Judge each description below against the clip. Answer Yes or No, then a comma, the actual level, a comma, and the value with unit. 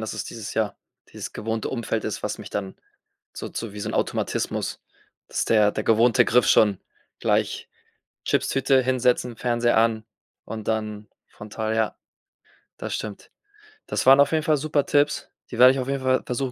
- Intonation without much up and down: No, average, 3.1 semitones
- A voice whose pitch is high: No, low, 115 Hz